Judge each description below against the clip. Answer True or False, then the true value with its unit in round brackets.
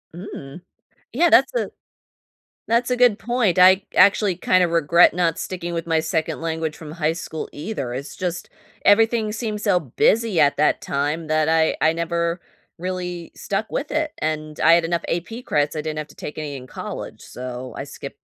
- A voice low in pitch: False (170 Hz)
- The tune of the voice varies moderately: True (4.6 semitones)